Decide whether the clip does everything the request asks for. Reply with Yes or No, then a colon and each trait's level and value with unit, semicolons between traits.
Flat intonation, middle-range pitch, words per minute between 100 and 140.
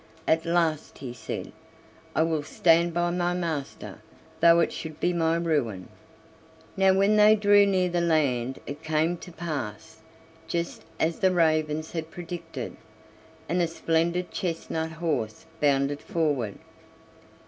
Yes: narrow, 2.2 semitones; medium, 165 Hz; slow, 135 wpm